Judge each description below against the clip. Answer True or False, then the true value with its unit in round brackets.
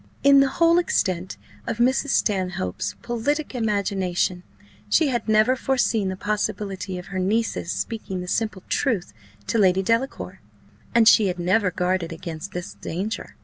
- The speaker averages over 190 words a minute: False (145 wpm)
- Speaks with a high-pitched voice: True (205 Hz)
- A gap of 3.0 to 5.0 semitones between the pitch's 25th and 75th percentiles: True (4.3 semitones)